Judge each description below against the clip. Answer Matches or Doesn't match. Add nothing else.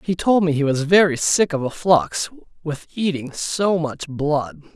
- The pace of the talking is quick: Doesn't match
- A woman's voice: Doesn't match